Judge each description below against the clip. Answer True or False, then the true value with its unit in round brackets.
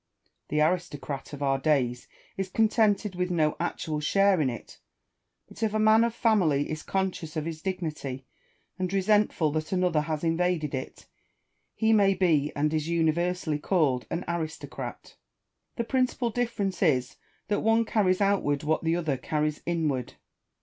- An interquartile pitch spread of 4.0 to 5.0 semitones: True (4.6 semitones)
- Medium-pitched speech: True (170 Hz)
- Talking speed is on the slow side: False (155 wpm)